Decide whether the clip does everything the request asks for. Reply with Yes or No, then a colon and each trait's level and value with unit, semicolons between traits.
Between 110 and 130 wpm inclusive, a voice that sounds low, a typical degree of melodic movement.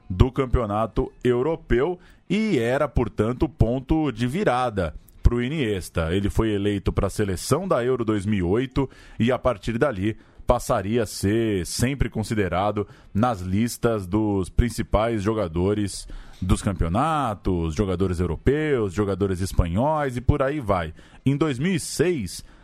Yes: average, 125 wpm; low, 110 Hz; average, 4.3 semitones